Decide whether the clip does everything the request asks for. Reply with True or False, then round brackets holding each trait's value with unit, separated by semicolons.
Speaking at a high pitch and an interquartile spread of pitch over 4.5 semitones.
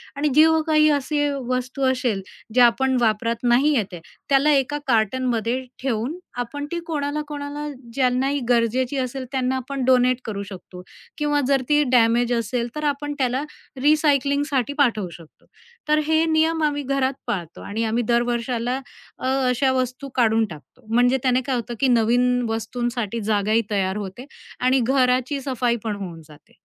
False (255 Hz; 3.4 semitones)